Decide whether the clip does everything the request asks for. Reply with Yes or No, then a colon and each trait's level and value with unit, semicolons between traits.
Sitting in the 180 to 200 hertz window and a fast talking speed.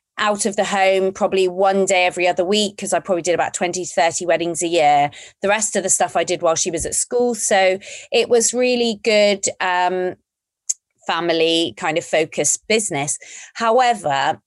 No: high, 190 Hz; average, 185 wpm